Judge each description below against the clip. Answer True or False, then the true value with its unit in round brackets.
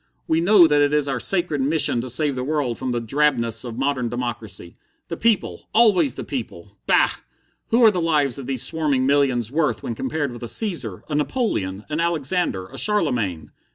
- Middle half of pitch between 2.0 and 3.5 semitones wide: False (5.1 semitones)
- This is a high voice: False (140 Hz)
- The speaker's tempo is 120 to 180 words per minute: False (190 wpm)